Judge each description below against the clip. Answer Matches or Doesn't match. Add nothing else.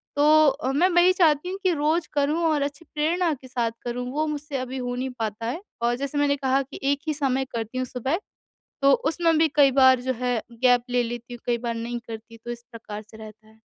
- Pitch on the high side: Matches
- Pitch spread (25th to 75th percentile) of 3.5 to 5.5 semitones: Matches